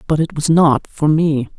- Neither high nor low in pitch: Yes, medium, 150 Hz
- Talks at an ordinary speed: No, fast, 225 wpm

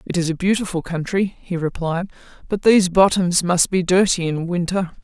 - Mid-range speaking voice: Yes, medium, 180 Hz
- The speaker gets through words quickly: No, average, 180 wpm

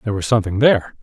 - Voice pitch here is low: Yes, low, 110 Hz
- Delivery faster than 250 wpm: No, fast, 235 wpm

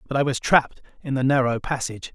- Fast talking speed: Yes, fast, 225 wpm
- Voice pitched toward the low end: Yes, low, 130 Hz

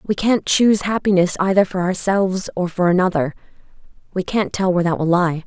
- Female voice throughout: Yes, female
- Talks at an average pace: Yes, average, 185 wpm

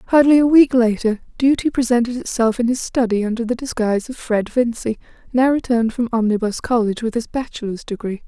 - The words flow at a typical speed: Yes, average, 180 wpm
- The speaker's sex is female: Yes, female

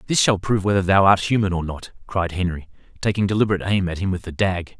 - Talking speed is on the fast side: Yes, fast, 240 wpm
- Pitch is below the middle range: Yes, very low, 95 Hz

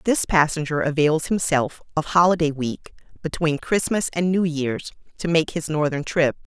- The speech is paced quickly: No, average, 155 wpm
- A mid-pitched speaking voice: Yes, medium, 160 Hz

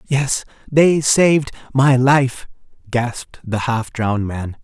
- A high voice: No, low, 130 Hz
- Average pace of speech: No, slow, 105 wpm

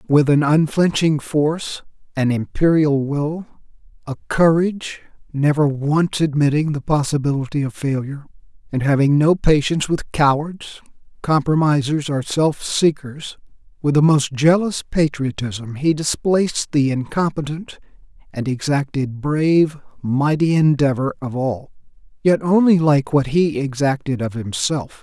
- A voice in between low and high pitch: Yes, medium, 145 Hz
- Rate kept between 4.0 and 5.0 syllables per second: Yes, 4.4 syllables/s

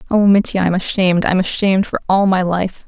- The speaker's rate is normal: No, fast, 210 wpm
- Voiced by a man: No, female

